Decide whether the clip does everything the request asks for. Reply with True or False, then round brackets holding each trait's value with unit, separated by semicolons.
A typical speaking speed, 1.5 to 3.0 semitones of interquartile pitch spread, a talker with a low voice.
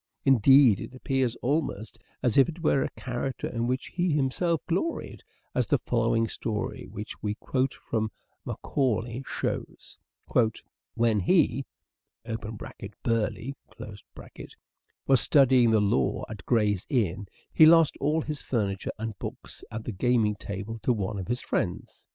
False (145 wpm; 4.0 semitones; 120 Hz)